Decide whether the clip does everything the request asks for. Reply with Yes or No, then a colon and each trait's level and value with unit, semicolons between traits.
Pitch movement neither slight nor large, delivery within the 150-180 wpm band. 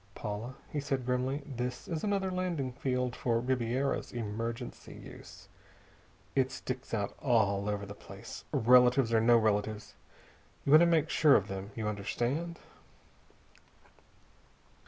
No: average, 4.0 semitones; slow, 135 wpm